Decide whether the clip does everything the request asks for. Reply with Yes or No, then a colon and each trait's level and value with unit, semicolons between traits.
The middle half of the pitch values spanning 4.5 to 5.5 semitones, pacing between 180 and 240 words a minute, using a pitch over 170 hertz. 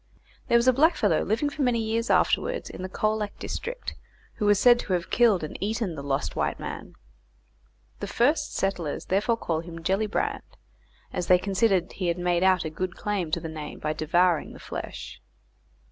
Yes: average, 4.8 semitones; average, 185 wpm; high, 190 Hz